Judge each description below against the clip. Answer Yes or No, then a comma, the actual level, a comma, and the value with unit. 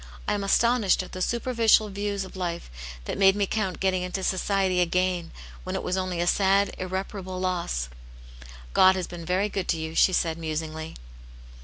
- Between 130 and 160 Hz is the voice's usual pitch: No, medium, 185 Hz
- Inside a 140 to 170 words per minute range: No, average, 185 wpm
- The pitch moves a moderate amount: No, narrow, 2.1 semitones